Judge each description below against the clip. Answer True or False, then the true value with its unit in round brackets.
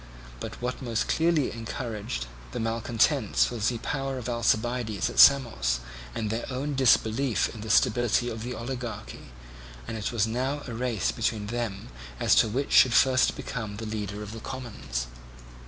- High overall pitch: False (115 Hz)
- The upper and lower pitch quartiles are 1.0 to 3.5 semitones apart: True (2.8 semitones)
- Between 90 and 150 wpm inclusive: False (165 wpm)